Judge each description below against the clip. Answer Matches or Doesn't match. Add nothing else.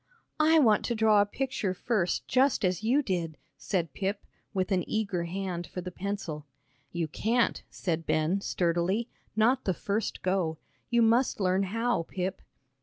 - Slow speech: Doesn't match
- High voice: Matches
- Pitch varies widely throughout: Doesn't match